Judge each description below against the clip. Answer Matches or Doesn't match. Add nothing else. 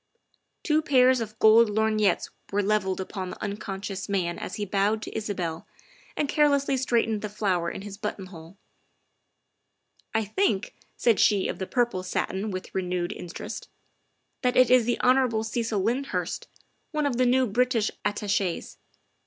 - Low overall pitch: Doesn't match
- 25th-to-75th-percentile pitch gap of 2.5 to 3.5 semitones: Doesn't match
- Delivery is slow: Doesn't match